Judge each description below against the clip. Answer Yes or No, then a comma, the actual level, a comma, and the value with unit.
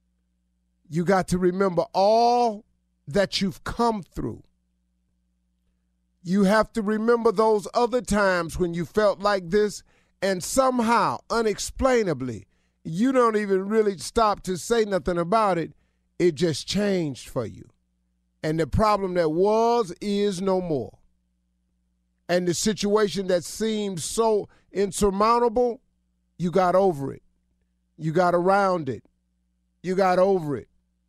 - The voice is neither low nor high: Yes, medium, 180 Hz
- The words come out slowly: Yes, slow, 125 wpm